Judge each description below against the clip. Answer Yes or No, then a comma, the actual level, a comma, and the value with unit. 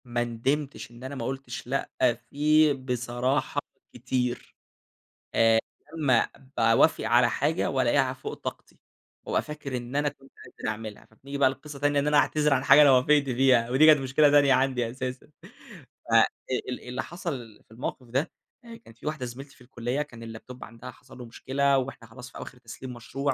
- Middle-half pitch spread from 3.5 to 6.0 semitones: No, average, 2.8 semitones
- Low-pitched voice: Yes, low, 130 Hz